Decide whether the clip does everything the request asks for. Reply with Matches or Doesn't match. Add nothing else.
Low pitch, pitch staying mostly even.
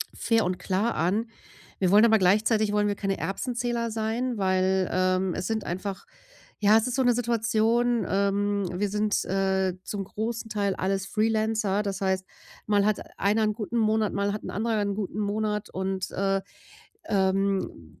Doesn't match